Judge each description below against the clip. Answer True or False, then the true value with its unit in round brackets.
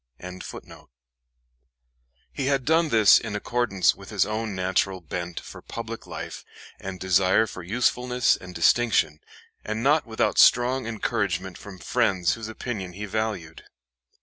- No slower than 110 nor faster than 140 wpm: True (135 wpm)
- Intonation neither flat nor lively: True (4.6 semitones)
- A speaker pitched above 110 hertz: False (105 Hz)